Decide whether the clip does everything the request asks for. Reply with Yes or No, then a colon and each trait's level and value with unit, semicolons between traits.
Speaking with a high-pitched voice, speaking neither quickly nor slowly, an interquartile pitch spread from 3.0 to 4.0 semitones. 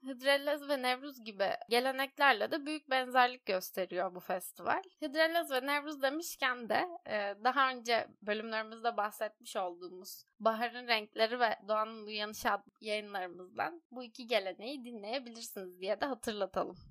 No: high, 235 Hz; average, 125 wpm; average, 4.4 semitones